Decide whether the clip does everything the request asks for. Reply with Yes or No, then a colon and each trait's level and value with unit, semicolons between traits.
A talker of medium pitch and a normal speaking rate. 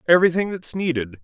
Yes: medium, 165 Hz; average, 145 wpm